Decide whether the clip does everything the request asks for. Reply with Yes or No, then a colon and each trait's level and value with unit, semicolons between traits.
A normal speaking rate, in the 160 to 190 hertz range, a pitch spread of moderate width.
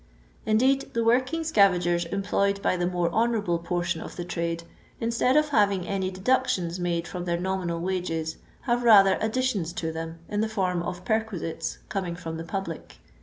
Yes: average, 170 wpm; medium, 185 Hz; average, 4.2 semitones